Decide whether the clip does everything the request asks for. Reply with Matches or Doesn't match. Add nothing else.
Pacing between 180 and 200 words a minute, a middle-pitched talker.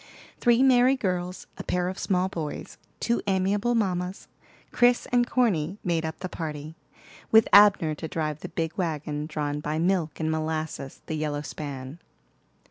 Doesn't match